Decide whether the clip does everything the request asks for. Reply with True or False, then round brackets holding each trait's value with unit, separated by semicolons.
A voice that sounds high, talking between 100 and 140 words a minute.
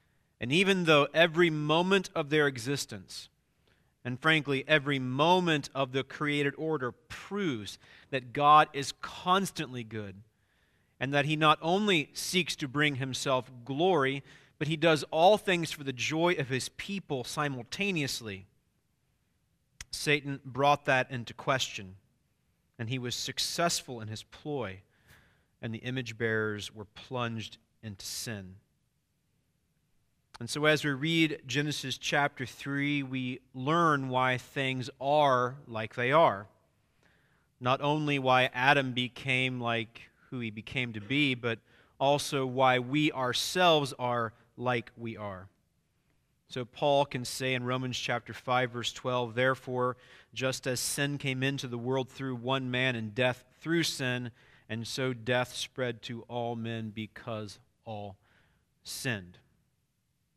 False (130 Hz; 135 wpm)